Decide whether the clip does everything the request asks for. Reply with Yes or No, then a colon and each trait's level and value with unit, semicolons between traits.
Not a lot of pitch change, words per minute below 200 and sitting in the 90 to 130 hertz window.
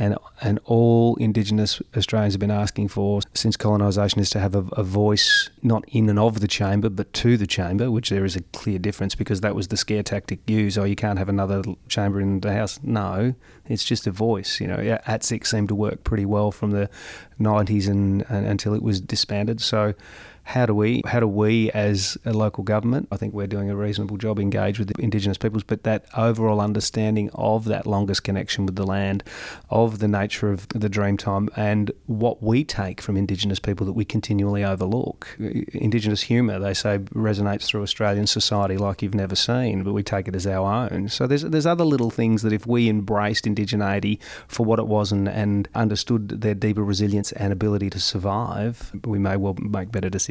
No: narrow, 1.6 semitones; fast, 205 wpm; low, 105 Hz